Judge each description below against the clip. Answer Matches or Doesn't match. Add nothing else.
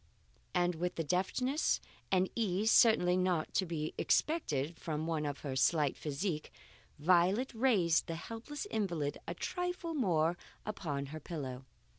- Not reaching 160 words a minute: Matches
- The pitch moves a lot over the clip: Matches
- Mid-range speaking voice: Matches